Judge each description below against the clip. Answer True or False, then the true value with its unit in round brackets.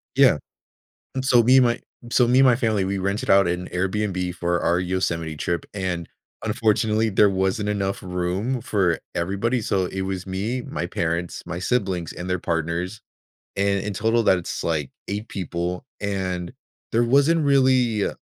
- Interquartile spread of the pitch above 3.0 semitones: True (3.9 semitones)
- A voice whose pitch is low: True (95 Hz)